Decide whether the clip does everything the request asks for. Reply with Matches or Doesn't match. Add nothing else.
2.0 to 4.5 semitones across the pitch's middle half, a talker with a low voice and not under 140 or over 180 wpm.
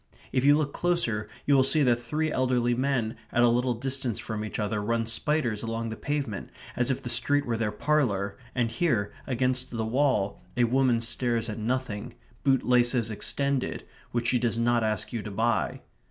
Doesn't match